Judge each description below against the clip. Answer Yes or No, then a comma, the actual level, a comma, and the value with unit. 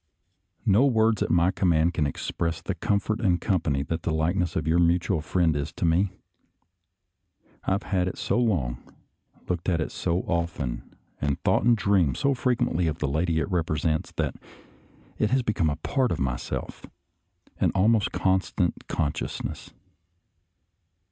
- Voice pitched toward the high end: No, very low, 85 Hz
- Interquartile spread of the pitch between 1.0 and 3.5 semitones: No, average, 4.0 semitones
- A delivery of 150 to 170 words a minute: Yes, average, 160 wpm